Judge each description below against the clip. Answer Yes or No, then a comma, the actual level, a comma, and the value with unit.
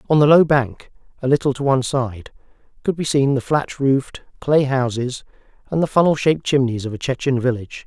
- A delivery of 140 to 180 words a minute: No, average, 200 wpm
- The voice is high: No, low, 135 Hz